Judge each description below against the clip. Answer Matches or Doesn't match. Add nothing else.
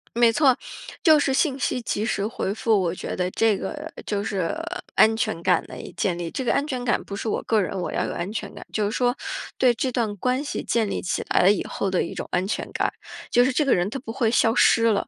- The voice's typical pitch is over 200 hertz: Matches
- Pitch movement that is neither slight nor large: Matches